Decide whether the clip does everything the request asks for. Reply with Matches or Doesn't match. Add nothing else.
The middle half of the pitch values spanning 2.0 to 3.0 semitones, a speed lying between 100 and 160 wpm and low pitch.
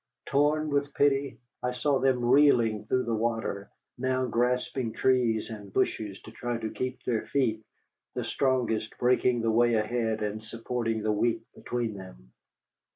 Matches